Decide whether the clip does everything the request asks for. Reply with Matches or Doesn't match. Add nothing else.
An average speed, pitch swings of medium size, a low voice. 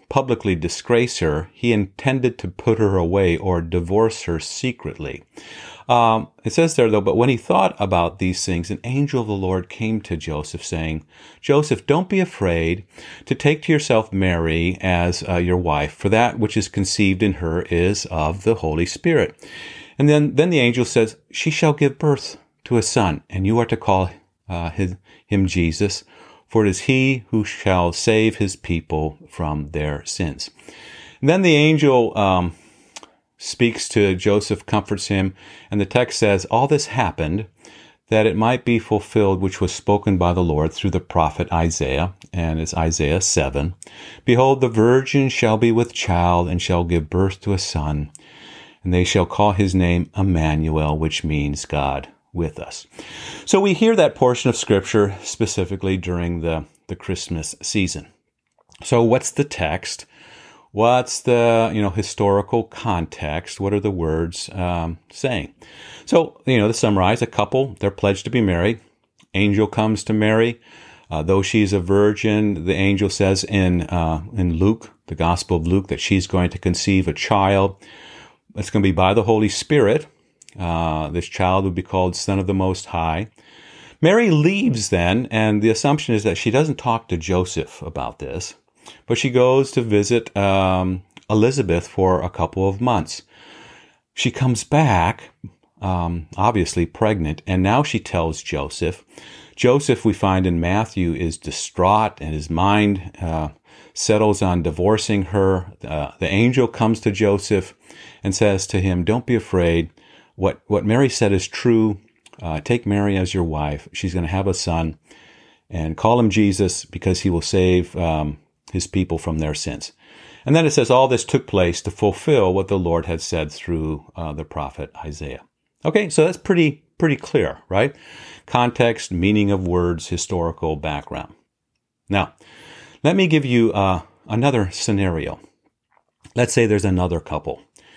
Matches